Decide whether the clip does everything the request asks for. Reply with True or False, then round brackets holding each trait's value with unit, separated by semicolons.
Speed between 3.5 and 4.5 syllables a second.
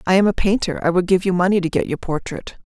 False (6.5 syllables/s)